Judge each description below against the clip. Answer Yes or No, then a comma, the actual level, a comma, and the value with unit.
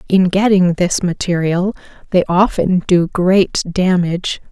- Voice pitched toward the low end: No, medium, 180 Hz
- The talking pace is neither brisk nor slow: No, slow, 120 wpm